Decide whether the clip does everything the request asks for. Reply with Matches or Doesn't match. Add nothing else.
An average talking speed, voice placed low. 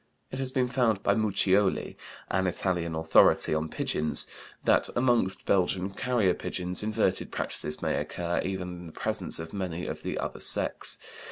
Matches